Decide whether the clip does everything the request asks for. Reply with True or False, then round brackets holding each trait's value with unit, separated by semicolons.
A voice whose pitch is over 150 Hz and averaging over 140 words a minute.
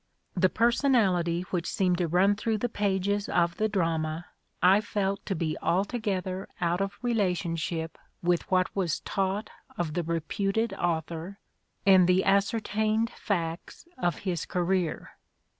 False (185 Hz; 135 wpm)